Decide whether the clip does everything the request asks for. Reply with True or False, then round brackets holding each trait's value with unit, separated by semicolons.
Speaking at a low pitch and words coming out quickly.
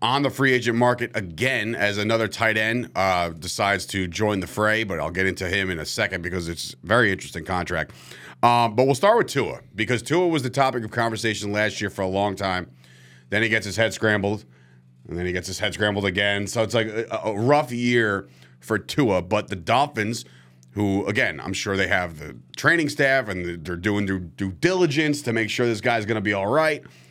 True (105 Hz; 225 wpm)